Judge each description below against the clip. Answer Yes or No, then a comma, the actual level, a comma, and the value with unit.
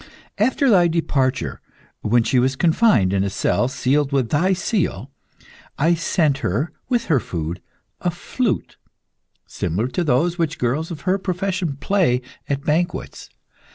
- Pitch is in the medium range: Yes, medium, 150 Hz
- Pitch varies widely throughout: Yes, wide, 5.9 semitones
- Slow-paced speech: No, average, 145 wpm